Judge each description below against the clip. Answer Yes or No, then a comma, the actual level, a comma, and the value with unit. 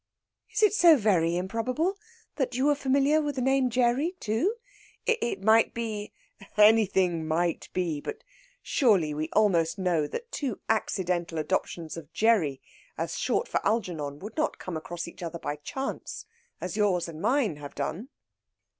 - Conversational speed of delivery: Yes, average, 165 wpm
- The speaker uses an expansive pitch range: Yes, wide, 7.3 semitones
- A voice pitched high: Yes, high, 210 Hz